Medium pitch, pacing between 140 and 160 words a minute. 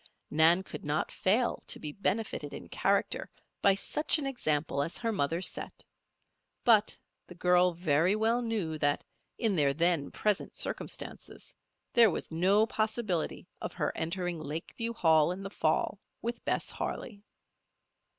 Yes: medium, 180 Hz; average, 145 wpm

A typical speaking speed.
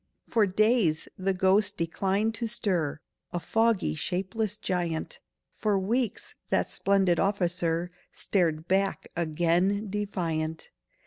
No: slow, 110 wpm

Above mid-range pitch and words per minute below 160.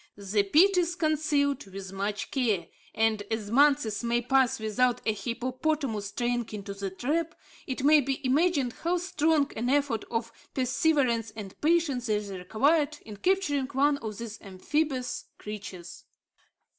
Yes: very high, 250 Hz; average, 145 wpm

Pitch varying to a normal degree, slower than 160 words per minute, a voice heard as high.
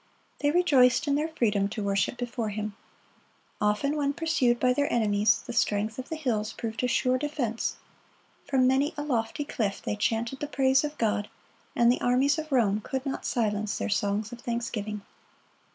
No: average, 4.8 semitones; average, 180 wpm; high, 240 Hz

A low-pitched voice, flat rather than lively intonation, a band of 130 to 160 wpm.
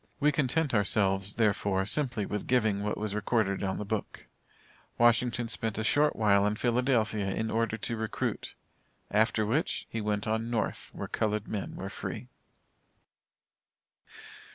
Yes: low, 110 Hz; narrow, 2.3 semitones; average, 145 wpm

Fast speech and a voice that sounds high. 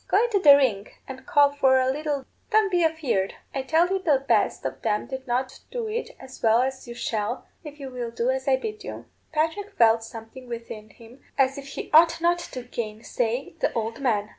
Yes: fast, 215 wpm; very high, 265 Hz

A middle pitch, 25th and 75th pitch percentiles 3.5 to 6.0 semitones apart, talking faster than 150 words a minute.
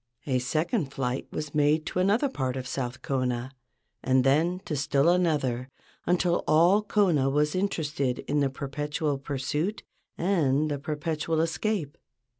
No: medium, 150 Hz; average, 3.9 semitones; average, 145 wpm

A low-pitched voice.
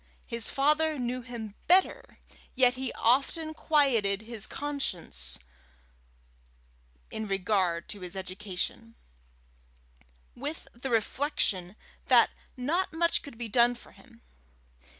No: high, 240 Hz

